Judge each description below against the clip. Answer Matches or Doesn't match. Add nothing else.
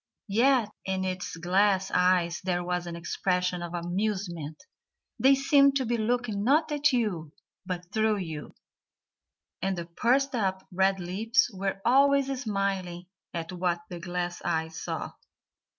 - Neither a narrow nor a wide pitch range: Matches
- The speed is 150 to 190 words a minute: Doesn't match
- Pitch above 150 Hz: Matches